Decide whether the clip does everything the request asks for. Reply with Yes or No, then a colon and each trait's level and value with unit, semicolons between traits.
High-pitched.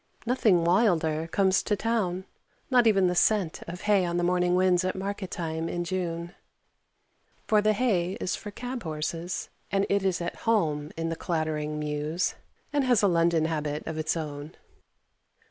No: medium, 175 Hz